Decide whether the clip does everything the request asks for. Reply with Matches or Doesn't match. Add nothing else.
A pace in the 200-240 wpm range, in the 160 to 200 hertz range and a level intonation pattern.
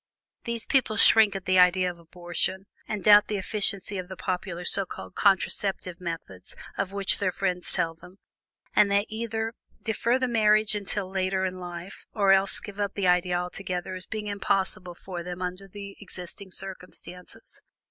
Doesn't match